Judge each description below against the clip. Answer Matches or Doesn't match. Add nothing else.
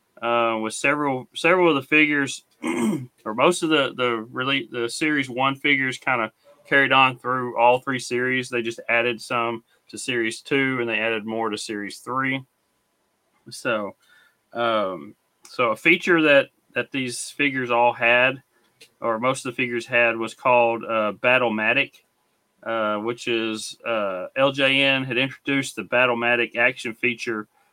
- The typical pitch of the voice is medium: Doesn't match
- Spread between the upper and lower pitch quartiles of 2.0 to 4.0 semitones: Matches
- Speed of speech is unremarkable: Matches